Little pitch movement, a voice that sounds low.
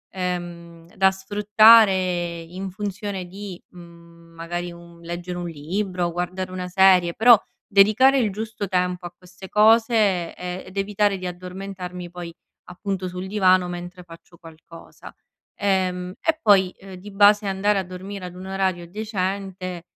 No: narrow, 2.1 semitones; medium, 185 Hz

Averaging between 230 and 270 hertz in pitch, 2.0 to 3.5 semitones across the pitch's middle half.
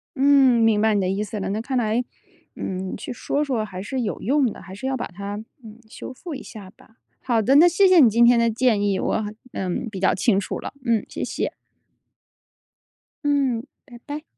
No: high, 235 Hz; average, 4.3 semitones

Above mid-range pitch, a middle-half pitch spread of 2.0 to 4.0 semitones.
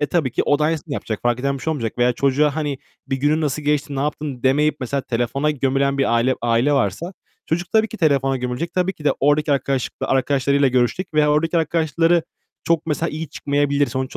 No: medium, 145 Hz; average, 2.7 semitones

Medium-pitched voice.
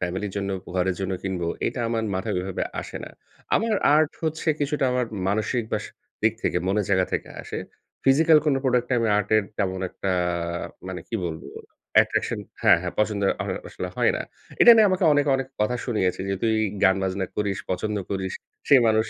No: low, 105 Hz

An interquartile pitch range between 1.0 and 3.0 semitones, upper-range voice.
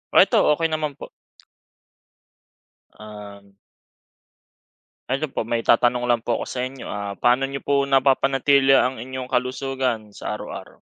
No: average, 2.7 semitones; low, 130 Hz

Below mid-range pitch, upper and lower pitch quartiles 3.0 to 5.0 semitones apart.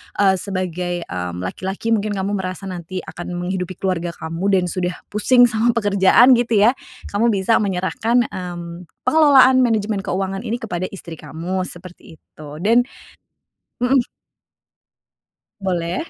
No: high, 190 Hz; average, 3.9 semitones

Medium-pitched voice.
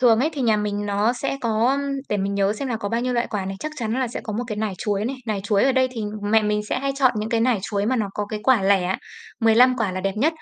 No: high, 220 Hz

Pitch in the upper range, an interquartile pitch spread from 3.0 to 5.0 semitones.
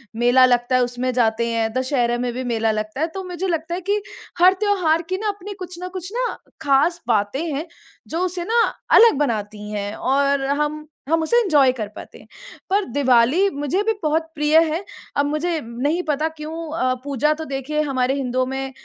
No: very high, 285 Hz; wide, 5.4 semitones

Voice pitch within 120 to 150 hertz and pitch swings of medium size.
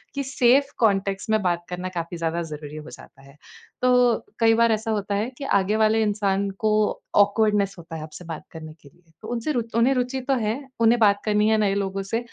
No: high, 210 Hz; average, 4.2 semitones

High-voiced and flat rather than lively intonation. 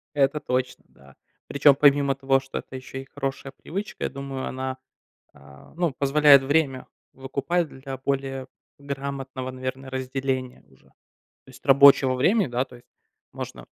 No: low, 135 Hz; narrow, 1.2 semitones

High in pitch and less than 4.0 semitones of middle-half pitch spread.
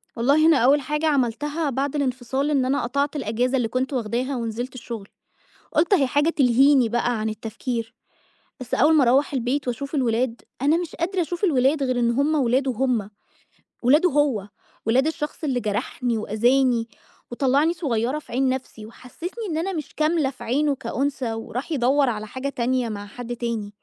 Yes: very high, 260 Hz; average, 3.6 semitones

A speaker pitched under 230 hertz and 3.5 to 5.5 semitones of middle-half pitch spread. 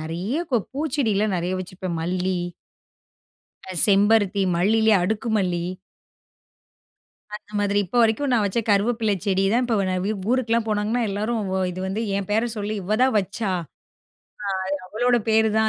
No: high, 210 Hz; average, 3.0 semitones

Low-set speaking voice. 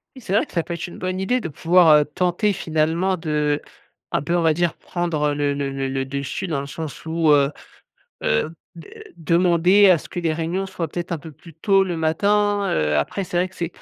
No: medium, 165 Hz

